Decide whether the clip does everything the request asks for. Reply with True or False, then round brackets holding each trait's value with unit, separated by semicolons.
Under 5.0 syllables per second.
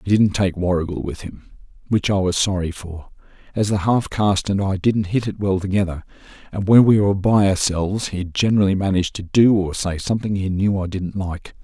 False (5.7 syllables/s)